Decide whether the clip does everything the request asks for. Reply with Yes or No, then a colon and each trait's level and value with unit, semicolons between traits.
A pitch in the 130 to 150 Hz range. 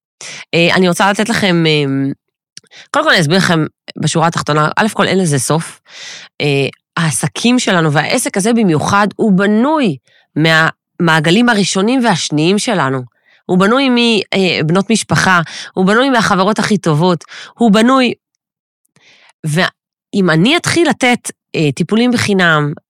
No: medium, 185 Hz